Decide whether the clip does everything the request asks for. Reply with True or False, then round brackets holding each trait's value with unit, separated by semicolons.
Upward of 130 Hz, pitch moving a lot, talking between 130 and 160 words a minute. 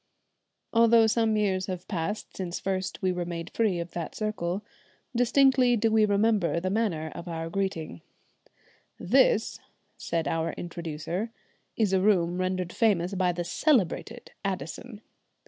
False (190 Hz; 4.2 semitones; 140 wpm)